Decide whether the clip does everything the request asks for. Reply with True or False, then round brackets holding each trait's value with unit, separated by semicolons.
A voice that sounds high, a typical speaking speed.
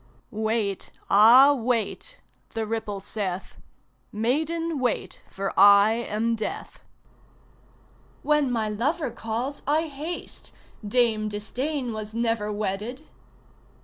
False (230 Hz; 100 wpm)